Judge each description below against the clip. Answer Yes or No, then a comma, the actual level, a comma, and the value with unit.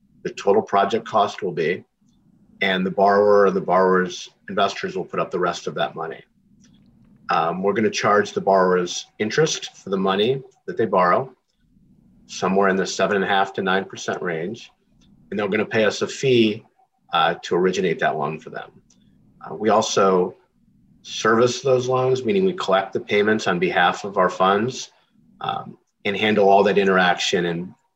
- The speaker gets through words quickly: No, average, 180 wpm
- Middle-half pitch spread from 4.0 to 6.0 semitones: Yes, average, 5.2 semitones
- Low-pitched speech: Yes, low, 105 Hz